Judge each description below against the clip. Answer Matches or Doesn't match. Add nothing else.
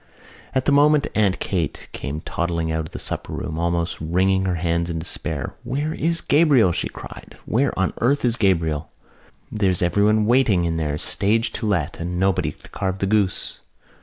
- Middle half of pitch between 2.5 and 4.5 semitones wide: Doesn't match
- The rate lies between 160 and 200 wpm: Matches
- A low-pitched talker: Matches